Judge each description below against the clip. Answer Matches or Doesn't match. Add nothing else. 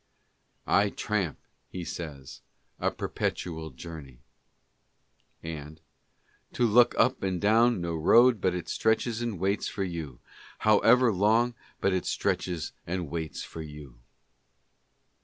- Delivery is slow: Matches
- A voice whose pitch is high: Doesn't match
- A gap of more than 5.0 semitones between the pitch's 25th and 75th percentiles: Matches